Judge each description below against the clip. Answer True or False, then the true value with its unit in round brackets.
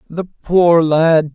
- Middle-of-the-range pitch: True (165 Hz)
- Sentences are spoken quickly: False (135 wpm)